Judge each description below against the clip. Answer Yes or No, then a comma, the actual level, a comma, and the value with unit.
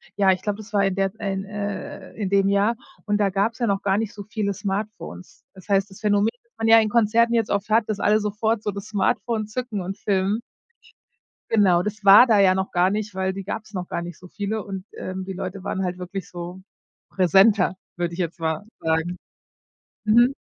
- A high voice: Yes, high, 200 Hz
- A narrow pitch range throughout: Yes, narrow, 2.2 semitones